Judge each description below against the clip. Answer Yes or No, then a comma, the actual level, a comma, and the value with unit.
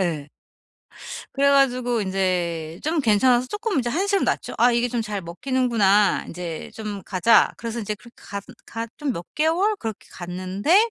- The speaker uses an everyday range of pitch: No, wide, 6.2 semitones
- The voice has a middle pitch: No, high, 230 Hz